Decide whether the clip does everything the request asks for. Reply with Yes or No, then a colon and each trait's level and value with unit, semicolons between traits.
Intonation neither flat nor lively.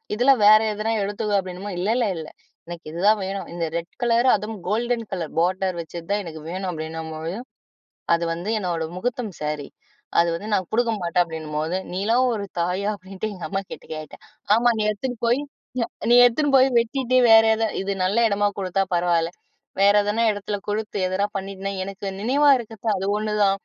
Yes: average, 4.1 semitones